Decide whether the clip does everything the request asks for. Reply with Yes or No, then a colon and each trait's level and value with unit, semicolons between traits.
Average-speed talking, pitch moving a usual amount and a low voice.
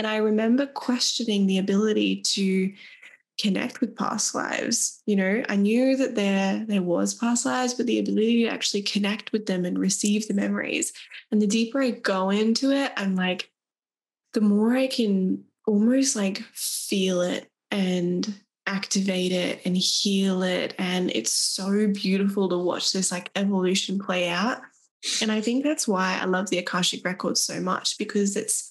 No: average, 170 wpm; average, 3.5 semitones; high, 205 Hz